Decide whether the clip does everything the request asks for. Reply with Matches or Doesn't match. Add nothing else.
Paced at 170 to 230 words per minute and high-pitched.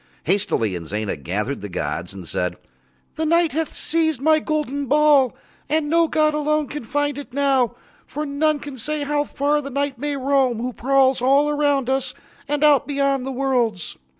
Matches